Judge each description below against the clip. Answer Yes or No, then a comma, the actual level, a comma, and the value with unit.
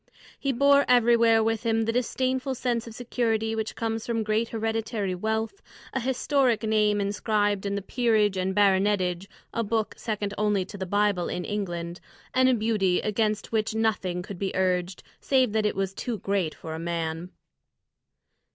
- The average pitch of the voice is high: Yes, high, 215 Hz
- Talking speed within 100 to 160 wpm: No, average, 170 wpm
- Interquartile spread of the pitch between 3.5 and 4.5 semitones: No, average, 2.9 semitones